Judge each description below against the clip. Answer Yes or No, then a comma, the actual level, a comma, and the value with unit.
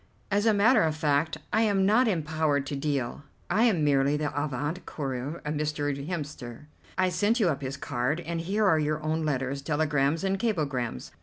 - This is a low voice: No, medium, 155 Hz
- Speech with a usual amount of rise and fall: Yes, average, 4.6 semitones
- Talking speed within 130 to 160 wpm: No, average, 185 wpm